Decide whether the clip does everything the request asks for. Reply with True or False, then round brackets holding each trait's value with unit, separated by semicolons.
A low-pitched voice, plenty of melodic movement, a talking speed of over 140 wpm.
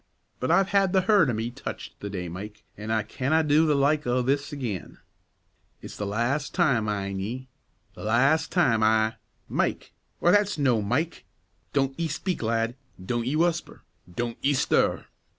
True (130 Hz; 6.0 semitones; 175 wpm)